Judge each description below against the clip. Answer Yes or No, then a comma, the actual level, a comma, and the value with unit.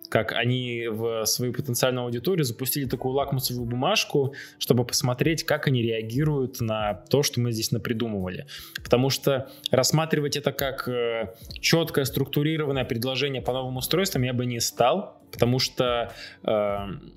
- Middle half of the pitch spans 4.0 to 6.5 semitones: No, average, 2.9 semitones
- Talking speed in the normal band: Yes, average, 135 wpm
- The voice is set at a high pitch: No, low, 130 Hz